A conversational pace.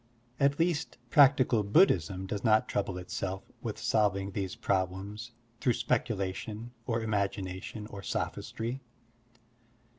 No: slow, 110 wpm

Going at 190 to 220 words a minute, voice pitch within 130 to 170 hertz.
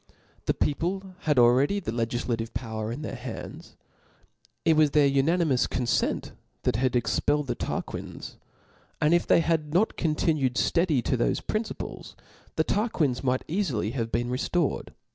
No: average, 155 wpm; medium, 140 Hz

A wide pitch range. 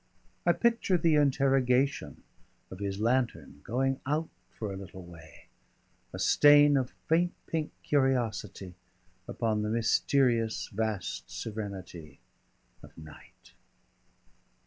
Yes: wide, 6.0 semitones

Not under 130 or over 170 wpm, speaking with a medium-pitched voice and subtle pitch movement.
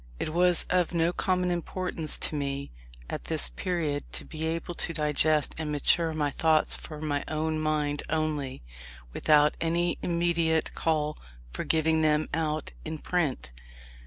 Yes: average, 150 wpm; medium, 155 Hz; narrow, 1.8 semitones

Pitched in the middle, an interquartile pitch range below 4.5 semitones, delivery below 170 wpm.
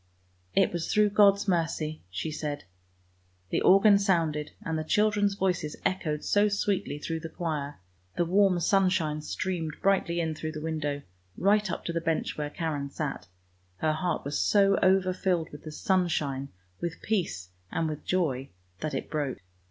No: medium, 165 Hz; average, 4.0 semitones; average, 175 wpm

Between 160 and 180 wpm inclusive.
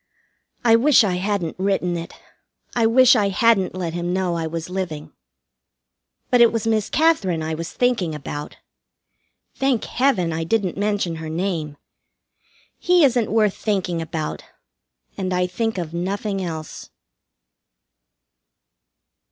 No: slow, 135 wpm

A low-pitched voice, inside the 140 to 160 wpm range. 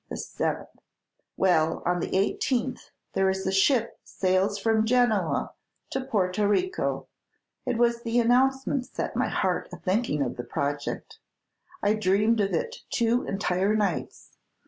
No: high, 210 Hz; average, 145 wpm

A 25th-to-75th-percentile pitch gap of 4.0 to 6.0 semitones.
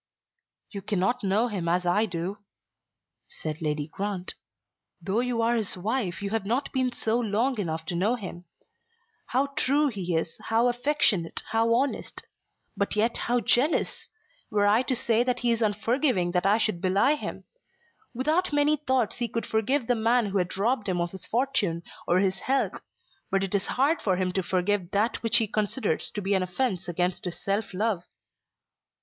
Yes: average, 4.7 semitones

